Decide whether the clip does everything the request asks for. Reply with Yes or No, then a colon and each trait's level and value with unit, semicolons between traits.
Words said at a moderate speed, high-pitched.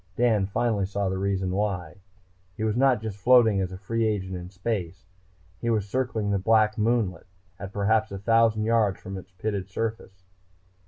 No: average, 175 wpm; low, 105 Hz